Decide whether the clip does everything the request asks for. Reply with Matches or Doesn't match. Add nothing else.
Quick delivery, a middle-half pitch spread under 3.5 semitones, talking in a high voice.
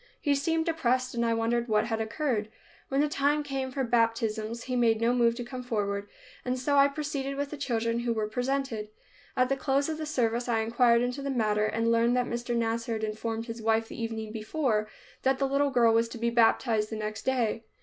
Matches